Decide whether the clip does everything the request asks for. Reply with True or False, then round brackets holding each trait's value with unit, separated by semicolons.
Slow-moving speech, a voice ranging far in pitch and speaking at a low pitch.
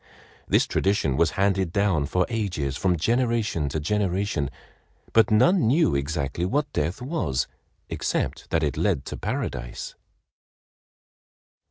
True (120 wpm; 7.0 semitones; 90 Hz)